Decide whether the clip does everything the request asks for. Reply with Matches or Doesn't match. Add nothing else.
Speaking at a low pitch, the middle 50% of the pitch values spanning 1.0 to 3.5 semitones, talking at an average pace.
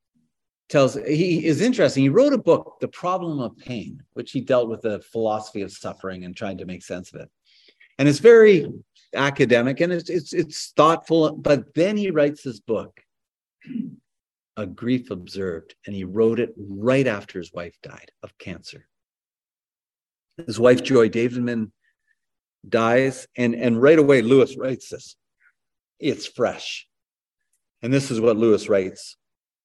Doesn't match